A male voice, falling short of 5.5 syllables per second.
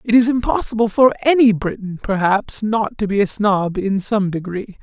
Yes: male; 4.8 syllables/s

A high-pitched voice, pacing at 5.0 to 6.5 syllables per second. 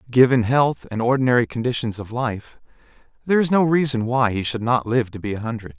No: low, 120 Hz; 5.9 syllables/s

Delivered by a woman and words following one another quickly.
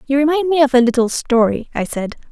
Yes: female; fast, 235 wpm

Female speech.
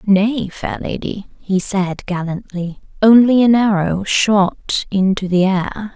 Yes: female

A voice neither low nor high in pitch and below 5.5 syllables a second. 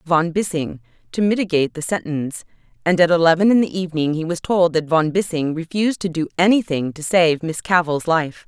No: medium, 170 Hz; 5.7 syllables/s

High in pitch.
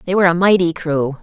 No: medium, 170 Hz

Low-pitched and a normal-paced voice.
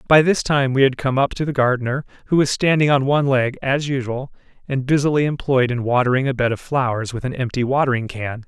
No: low, 130 Hz; fast, 225 wpm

